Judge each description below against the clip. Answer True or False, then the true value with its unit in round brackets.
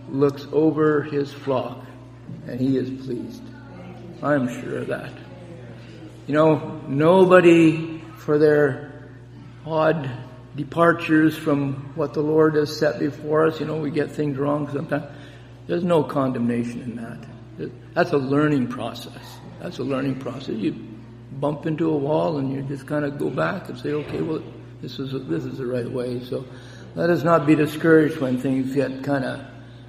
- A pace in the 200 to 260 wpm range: False (165 wpm)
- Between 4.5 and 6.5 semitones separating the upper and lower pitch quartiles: False (3.4 semitones)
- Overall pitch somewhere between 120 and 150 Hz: True (140 Hz)